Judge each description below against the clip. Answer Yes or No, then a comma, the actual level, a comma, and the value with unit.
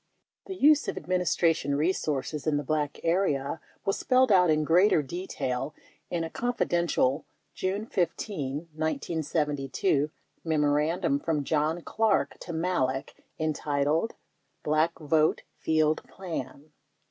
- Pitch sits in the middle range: Yes, medium, 160 Hz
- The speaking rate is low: Yes, slow, 115 wpm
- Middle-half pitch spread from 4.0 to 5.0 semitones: No, average, 3.5 semitones